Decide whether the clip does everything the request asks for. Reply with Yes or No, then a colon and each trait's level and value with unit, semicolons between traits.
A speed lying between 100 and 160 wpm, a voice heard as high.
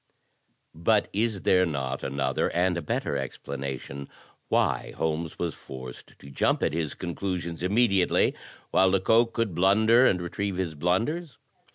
No: average, 140 wpm; very low, 90 Hz